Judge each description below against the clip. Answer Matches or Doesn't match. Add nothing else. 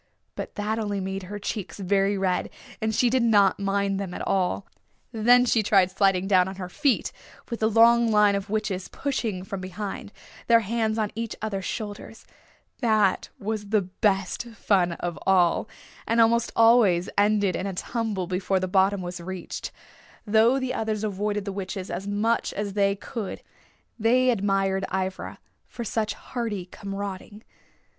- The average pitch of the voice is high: Matches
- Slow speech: Doesn't match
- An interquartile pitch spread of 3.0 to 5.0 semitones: Doesn't match